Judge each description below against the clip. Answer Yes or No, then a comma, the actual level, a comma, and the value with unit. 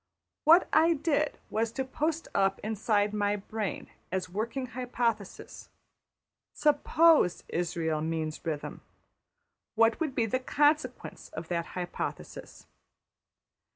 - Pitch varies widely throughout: Yes, wide, 7.8 semitones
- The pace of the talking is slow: Yes, slow, 115 wpm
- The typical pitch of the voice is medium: No, high, 225 Hz